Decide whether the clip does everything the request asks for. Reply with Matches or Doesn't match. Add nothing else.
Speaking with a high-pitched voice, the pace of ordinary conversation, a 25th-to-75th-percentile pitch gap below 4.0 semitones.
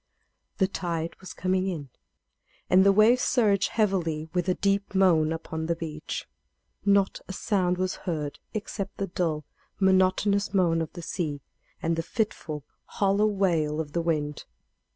Doesn't match